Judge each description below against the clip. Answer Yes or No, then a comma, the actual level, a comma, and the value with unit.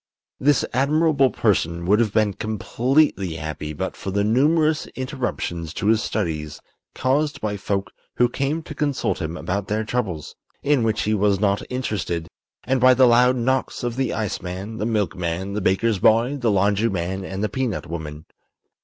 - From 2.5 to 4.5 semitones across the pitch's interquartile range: No, average, 5.2 semitones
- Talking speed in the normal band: Yes, average, 165 wpm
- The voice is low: Yes, low, 110 Hz